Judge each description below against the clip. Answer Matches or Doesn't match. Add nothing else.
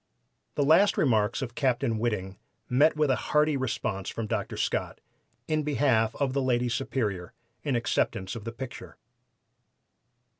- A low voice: Matches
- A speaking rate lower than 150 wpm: Matches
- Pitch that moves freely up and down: Doesn't match